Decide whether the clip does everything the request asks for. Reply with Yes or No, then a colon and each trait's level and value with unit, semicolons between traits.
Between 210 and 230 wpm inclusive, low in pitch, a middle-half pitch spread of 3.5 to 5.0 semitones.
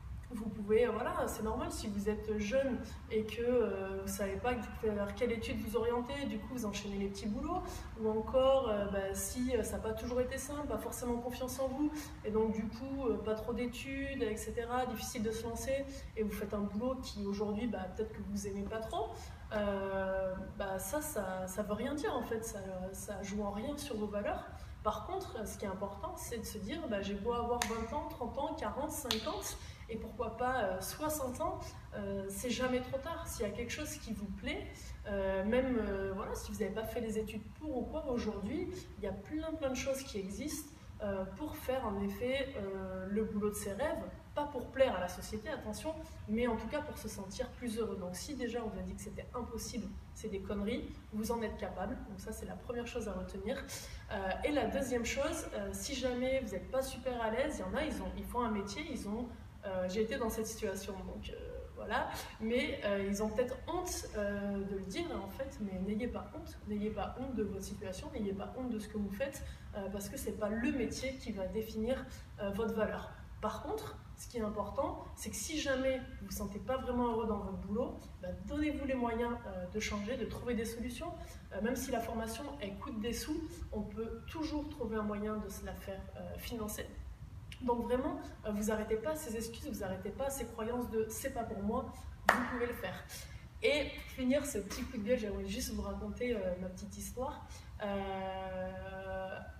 No: fast, 220 wpm; high, 225 Hz; average, 3.8 semitones